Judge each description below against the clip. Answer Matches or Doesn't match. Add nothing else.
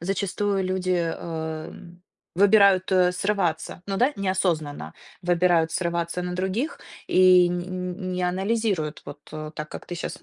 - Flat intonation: Matches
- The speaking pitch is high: Doesn't match